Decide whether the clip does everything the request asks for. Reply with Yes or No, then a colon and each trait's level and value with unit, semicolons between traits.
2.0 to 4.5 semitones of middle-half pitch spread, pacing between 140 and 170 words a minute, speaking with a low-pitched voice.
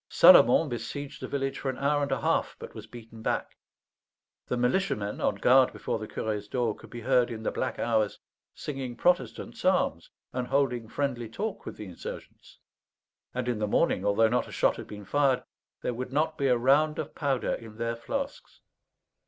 No: average, 3.8 semitones; average, 190 wpm; low, 125 Hz